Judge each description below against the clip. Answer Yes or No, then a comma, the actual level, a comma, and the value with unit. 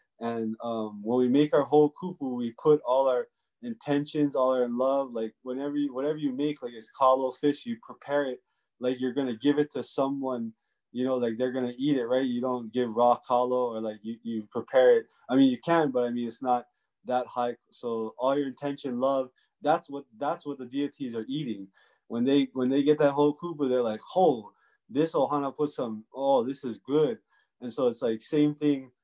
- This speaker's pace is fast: Yes, fast, 215 wpm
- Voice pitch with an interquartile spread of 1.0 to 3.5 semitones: Yes, average, 3.0 semitones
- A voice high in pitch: No, low, 130 Hz